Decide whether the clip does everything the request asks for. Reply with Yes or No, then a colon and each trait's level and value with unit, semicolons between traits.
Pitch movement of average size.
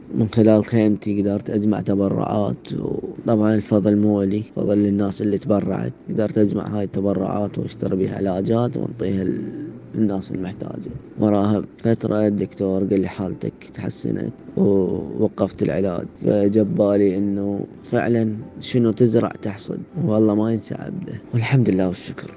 No: narrow, 1.6 semitones